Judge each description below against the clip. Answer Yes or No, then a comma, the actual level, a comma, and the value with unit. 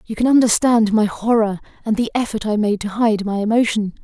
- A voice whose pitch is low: No, high, 220 Hz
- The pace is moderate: No, fast, 210 wpm